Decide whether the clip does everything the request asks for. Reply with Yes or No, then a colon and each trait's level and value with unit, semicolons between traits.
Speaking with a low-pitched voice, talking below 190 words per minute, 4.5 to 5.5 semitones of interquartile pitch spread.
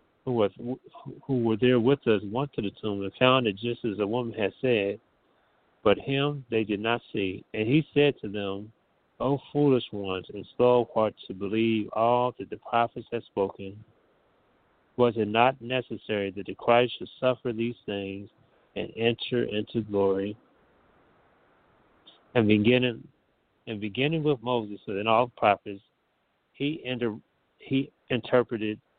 No: low, 115 Hz; average, 155 wpm; average, 3.2 semitones